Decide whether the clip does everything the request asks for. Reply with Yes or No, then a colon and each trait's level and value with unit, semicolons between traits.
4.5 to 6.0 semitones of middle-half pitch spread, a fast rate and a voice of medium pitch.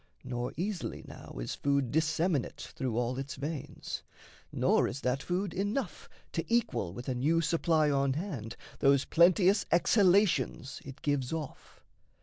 No: average, 5.1 semitones; average, 140 wpm; medium, 150 Hz